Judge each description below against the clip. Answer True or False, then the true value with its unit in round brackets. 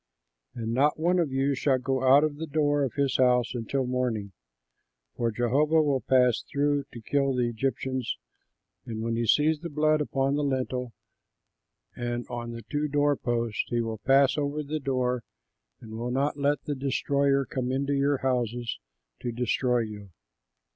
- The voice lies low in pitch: True (130 Hz)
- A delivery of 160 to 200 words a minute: True (170 wpm)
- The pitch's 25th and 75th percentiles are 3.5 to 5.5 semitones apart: False (3.0 semitones)